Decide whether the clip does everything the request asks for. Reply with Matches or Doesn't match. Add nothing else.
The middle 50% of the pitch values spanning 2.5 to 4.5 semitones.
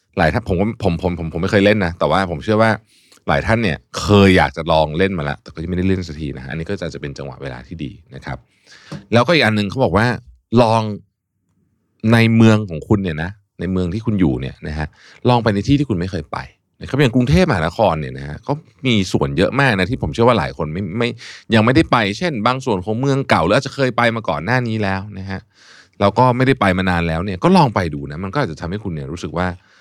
Doesn't match